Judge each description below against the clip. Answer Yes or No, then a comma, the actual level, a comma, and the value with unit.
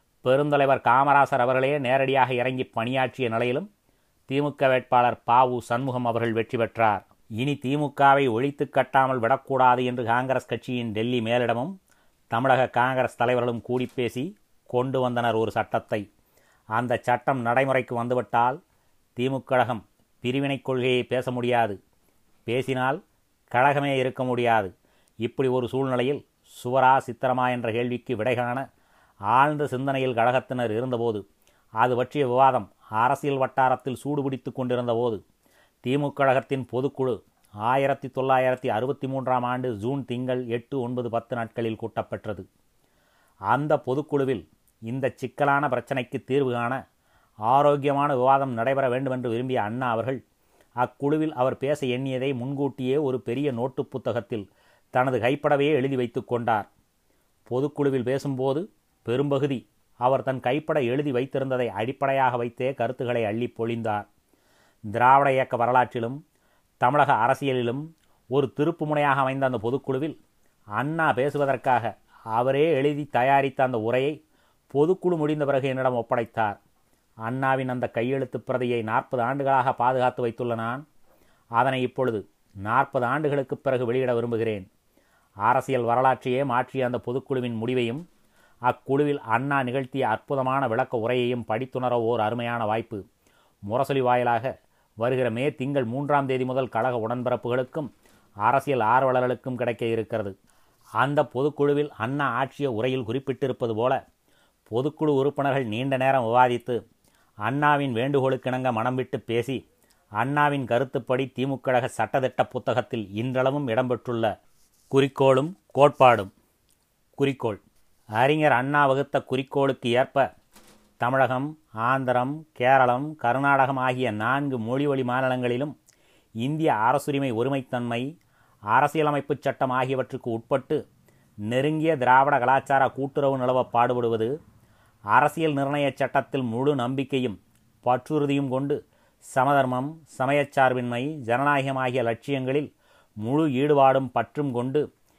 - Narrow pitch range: Yes, narrow, 2.3 semitones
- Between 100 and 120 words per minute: Yes, average, 105 wpm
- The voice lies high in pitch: No, low, 130 Hz